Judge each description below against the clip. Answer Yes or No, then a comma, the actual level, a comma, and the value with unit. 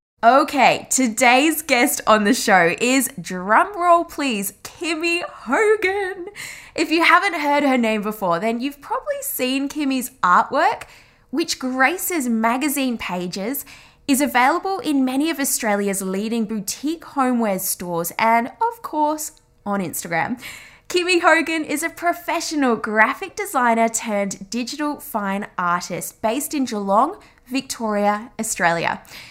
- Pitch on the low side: No, very high, 260 Hz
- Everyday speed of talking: No, slow, 120 wpm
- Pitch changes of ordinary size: No, wide, 6.5 semitones